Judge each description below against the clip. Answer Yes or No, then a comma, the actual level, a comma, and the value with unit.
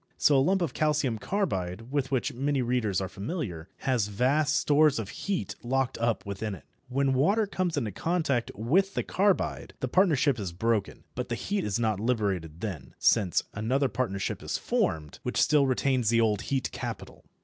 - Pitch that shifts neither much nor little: No, wide, 6.0 semitones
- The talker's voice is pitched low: Yes, low, 125 Hz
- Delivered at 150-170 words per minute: No, average, 180 wpm